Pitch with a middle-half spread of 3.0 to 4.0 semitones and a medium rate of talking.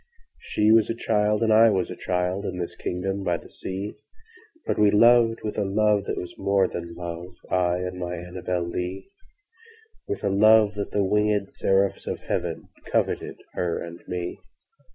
Yes: average, 3.3 semitones; average, 155 wpm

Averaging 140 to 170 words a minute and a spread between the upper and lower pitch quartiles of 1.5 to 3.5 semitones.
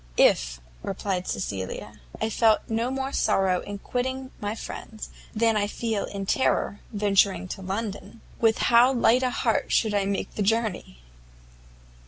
Yes: average, 150 wpm; average, 3.1 semitones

